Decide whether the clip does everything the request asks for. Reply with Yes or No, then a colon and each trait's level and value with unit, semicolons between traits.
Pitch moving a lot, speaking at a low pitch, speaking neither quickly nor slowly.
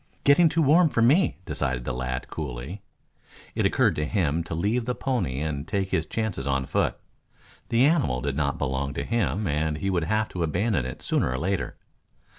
Yes: wide, 8.5 semitones; very low, 85 Hz; average, 195 wpm